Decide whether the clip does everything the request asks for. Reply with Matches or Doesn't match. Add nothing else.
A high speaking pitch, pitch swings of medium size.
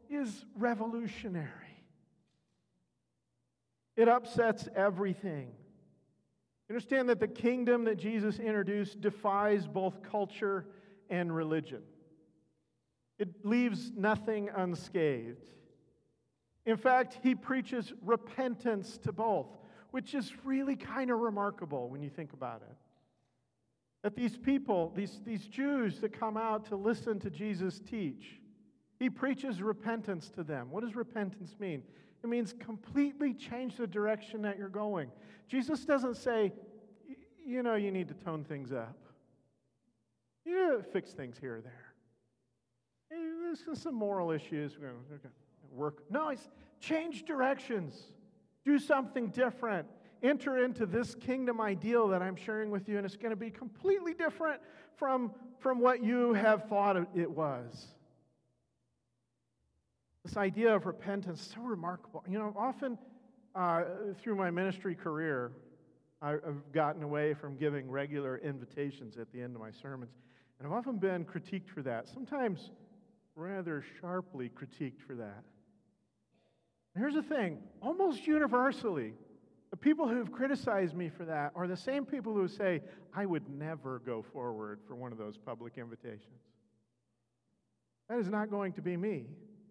Doesn't match